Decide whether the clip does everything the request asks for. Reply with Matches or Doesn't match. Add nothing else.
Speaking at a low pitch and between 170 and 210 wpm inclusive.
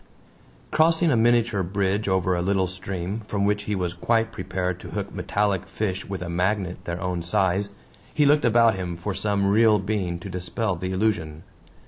Matches